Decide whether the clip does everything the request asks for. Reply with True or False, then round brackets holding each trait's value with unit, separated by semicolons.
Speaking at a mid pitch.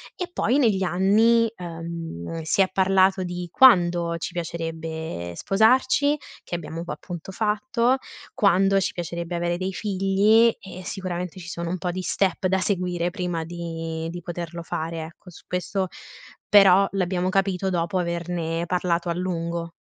True (180 Hz)